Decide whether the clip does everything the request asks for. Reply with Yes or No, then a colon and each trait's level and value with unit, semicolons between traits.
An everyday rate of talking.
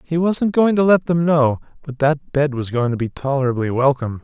No: fast, 225 wpm